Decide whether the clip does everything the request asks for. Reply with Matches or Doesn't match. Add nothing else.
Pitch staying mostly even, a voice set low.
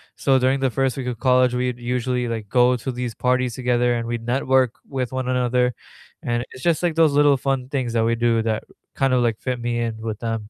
Matches